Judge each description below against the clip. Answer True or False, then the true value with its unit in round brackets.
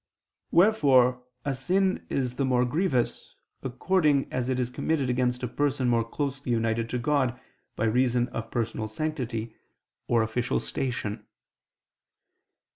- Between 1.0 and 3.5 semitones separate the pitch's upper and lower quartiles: True (2.9 semitones)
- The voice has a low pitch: True (125 Hz)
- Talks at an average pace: False (130 wpm)